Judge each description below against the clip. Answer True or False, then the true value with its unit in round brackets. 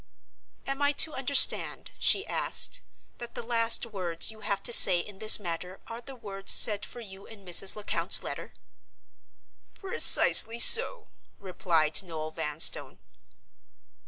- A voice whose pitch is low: False (210 Hz)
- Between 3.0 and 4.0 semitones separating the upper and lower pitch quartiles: False (4.8 semitones)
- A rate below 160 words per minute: True (135 wpm)